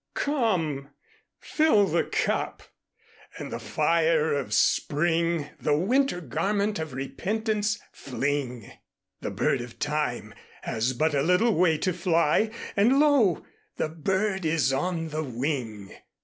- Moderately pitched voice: Yes, medium, 165 Hz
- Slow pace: Yes, slow, 130 wpm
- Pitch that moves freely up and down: Yes, wide, 5.8 semitones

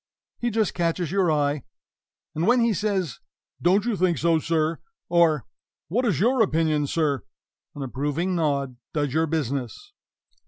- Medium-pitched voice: Yes, medium, 165 Hz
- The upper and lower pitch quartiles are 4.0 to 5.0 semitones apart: Yes, average, 4.7 semitones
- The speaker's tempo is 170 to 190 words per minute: No, average, 150 wpm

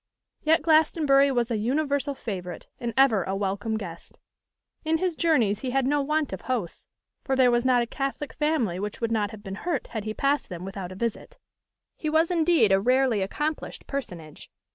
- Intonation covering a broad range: Yes, wide, 6.3 semitones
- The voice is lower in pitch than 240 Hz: No, very high, 250 Hz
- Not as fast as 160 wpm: No, average, 190 wpm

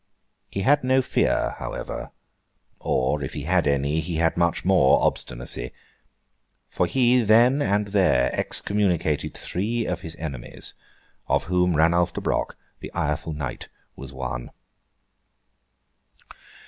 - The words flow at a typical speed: No, slow, 120 wpm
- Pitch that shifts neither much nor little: No, wide, 5.9 semitones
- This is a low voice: Yes, very low, 85 Hz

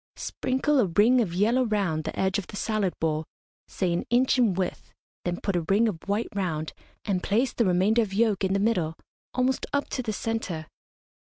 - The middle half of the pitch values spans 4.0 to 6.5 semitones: Yes, average, 4.4 semitones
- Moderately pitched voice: No, high, 205 Hz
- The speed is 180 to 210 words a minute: Yes, average, 200 wpm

